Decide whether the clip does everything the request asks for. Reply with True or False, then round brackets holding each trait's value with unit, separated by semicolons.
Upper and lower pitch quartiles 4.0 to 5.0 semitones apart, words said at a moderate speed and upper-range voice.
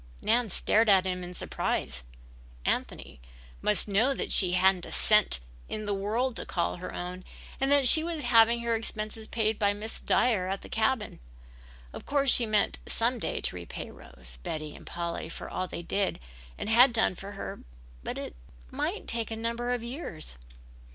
True (4.3 semitones; 180 wpm; 215 Hz)